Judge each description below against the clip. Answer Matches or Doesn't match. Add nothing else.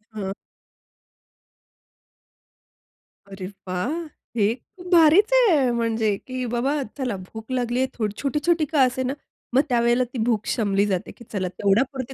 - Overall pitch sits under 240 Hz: Doesn't match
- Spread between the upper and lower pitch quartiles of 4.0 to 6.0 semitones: Matches